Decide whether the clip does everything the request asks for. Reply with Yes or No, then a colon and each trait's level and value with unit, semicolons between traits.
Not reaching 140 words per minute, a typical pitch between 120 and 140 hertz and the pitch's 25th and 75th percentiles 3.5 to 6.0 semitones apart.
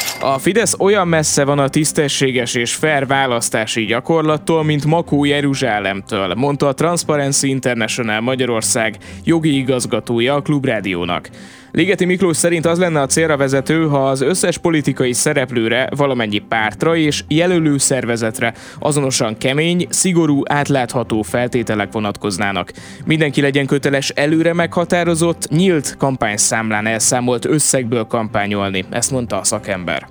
Yes: average, 120 wpm; low, 135 Hz; average, 5.0 semitones